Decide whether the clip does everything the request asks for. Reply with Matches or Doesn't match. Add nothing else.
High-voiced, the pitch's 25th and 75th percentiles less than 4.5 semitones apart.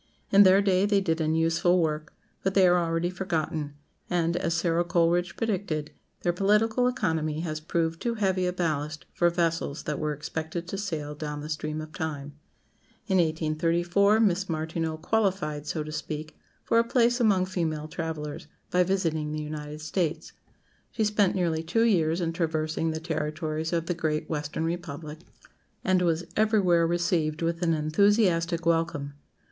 Doesn't match